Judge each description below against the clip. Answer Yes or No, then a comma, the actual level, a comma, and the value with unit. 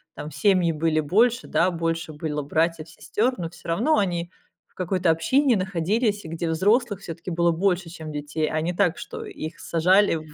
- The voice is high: No, medium, 170 Hz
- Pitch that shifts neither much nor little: Yes, average, 3.8 semitones